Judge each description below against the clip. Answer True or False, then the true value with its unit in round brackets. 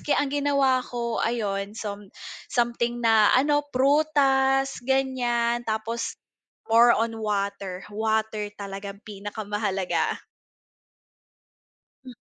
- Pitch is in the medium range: False (230 Hz)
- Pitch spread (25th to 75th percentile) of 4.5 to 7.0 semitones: False (4.1 semitones)